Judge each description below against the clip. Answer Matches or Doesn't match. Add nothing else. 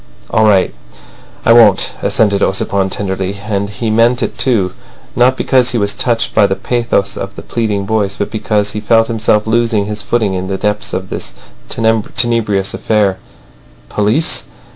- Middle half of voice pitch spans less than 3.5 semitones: Matches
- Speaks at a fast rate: Doesn't match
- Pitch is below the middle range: Matches